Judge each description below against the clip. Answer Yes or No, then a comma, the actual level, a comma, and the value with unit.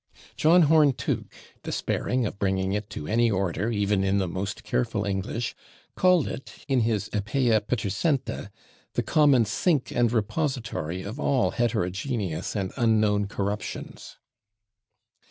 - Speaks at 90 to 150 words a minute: Yes, slow, 135 wpm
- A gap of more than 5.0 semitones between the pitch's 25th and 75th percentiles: No, average, 4.3 semitones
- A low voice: Yes, low, 110 Hz